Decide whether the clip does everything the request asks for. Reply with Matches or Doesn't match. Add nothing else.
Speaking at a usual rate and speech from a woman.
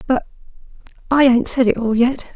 Matches